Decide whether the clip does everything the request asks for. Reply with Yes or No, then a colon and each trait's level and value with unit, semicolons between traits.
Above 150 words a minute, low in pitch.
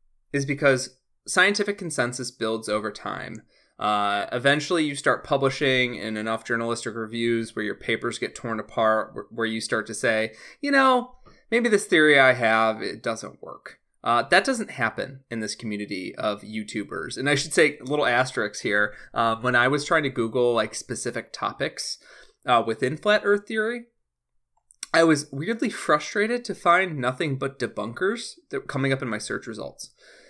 Yes: average, 170 wpm; low, 130 Hz